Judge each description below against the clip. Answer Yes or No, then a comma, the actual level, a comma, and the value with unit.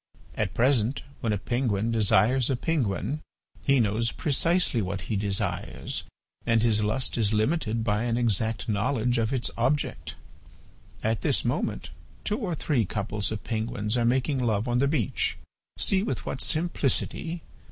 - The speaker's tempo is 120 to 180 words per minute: Yes, average, 150 wpm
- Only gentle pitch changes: No, average, 4.0 semitones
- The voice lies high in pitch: No, low, 115 Hz